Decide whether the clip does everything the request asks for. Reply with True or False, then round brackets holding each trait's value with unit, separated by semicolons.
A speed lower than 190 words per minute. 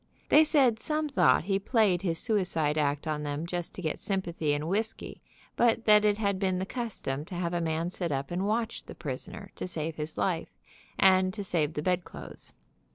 False (200 wpm)